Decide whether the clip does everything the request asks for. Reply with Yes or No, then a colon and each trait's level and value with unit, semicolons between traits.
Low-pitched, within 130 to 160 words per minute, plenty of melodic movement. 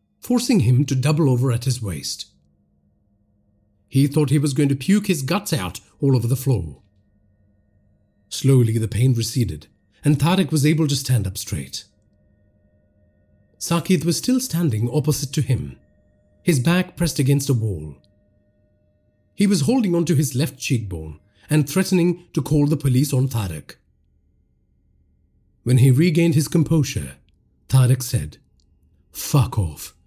Yes: low, 115 Hz; average, 140 wpm; wide, 6.8 semitones